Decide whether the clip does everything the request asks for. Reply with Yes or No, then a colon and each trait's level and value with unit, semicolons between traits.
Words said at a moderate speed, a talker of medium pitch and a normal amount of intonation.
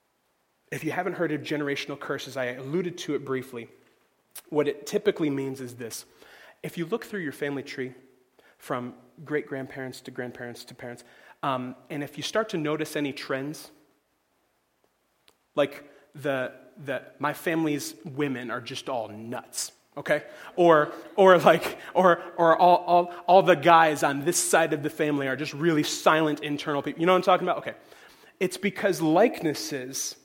Yes: average, 165 wpm; medium, 150 Hz; average, 3.9 semitones